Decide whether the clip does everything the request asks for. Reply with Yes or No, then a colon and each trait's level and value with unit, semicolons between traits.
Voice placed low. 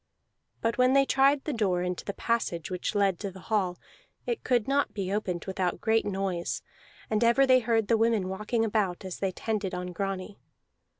No: high, 205 Hz